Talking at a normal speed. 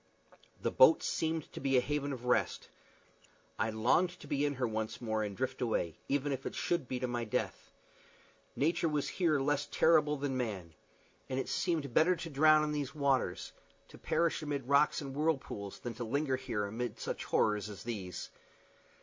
Yes: average, 185 wpm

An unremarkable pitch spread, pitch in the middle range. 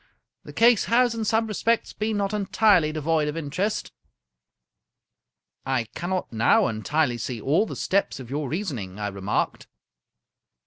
No: wide, 8.6 semitones; medium, 160 Hz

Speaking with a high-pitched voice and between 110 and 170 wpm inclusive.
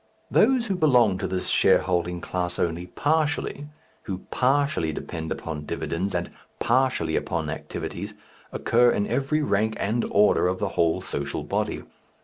No: low, 100 Hz; average, 140 wpm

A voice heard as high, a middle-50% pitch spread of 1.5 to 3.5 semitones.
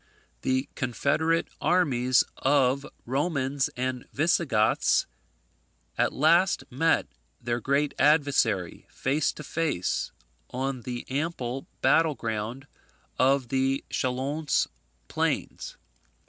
No: low, 135 Hz; average, 3.0 semitones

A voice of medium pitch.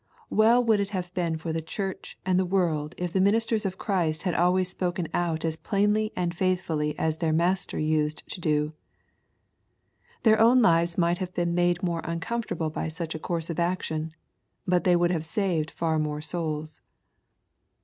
Yes: medium, 175 Hz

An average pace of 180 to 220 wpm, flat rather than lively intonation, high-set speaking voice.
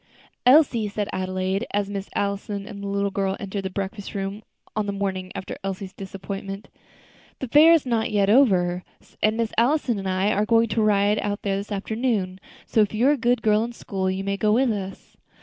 Yes: fast, 205 wpm; narrow, 2.2 semitones; high, 200 Hz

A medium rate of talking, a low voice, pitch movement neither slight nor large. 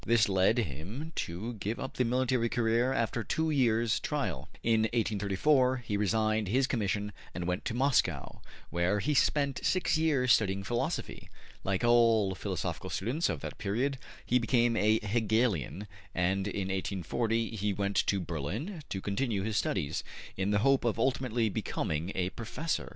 Yes: average, 155 wpm; low, 110 Hz; average, 4.0 semitones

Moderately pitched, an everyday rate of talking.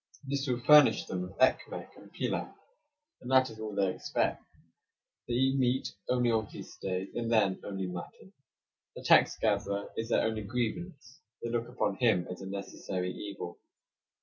No: low, 115 Hz; average, 170 wpm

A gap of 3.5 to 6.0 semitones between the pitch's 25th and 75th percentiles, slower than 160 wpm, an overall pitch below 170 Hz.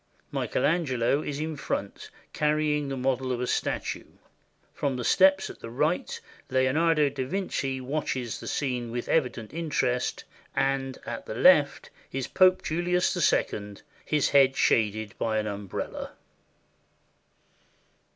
Yes: average, 3.8 semitones; average, 140 wpm; low, 135 Hz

